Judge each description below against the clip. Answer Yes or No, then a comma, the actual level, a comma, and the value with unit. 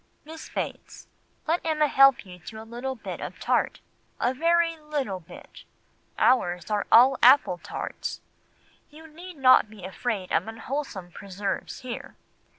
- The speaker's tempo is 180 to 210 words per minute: No, average, 140 wpm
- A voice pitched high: Yes, very high, 255 Hz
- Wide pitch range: Yes, wide, 6.7 semitones